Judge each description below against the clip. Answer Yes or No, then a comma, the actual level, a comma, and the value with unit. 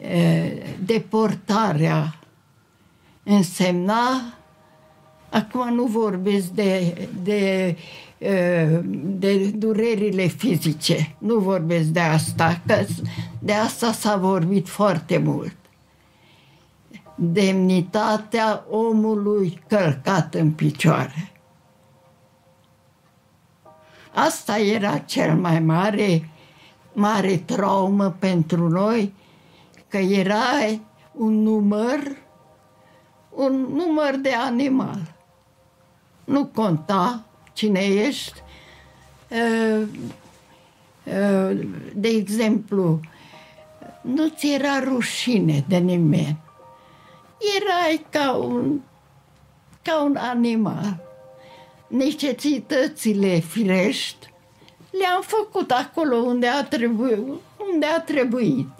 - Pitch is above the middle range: Yes, high, 200 Hz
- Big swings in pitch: Yes, wide, 5.8 semitones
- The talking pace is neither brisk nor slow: No, slow, 75 wpm